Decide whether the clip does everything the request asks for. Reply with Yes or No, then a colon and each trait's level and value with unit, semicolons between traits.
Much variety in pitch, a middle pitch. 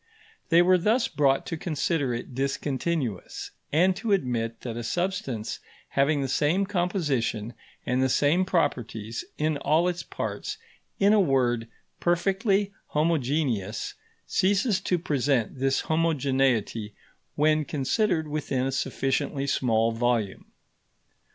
Yes: wide, 5.7 semitones; medium, 145 Hz